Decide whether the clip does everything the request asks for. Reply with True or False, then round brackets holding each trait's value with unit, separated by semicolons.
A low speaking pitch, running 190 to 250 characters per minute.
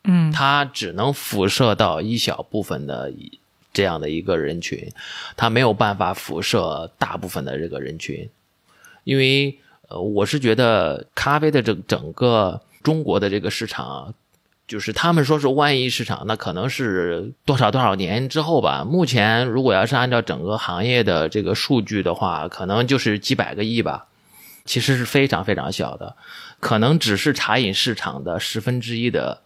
False (115 Hz; 260 characters per minute)